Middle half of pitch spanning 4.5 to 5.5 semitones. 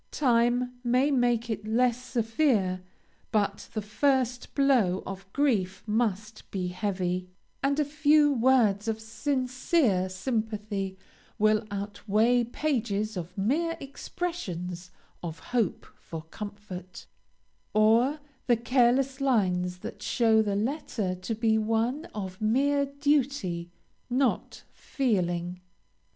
Yes: average, 5.0 semitones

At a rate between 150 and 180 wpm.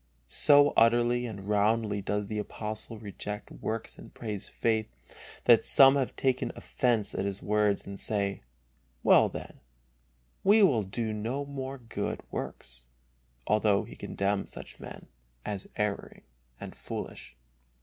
No: slow, 135 wpm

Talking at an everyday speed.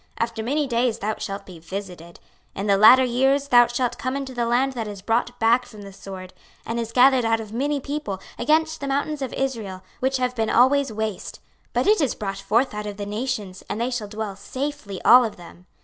No: fast, 225 wpm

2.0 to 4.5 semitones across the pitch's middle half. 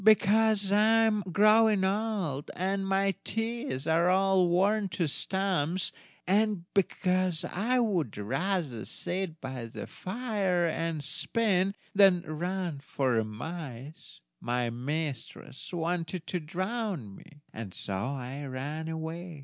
No: average, 5.2 semitones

